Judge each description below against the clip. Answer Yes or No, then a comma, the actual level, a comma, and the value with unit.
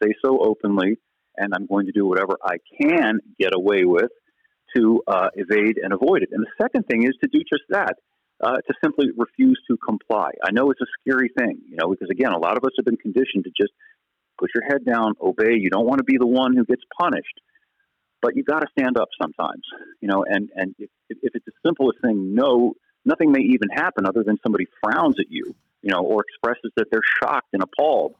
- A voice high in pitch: No, medium, 140 Hz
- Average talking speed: No, fast, 225 wpm